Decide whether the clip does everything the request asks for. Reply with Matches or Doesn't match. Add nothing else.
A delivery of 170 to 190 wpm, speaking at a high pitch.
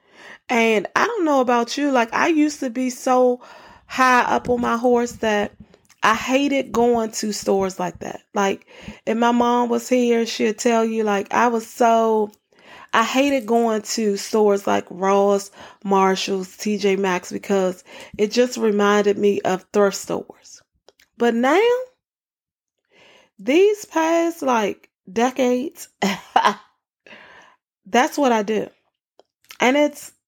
Doesn't match